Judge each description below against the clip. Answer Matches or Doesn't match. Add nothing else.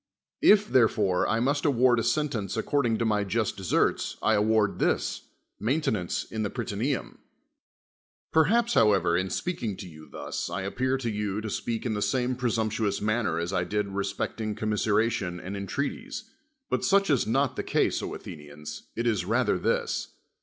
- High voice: Doesn't match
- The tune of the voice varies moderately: Matches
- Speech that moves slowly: Doesn't match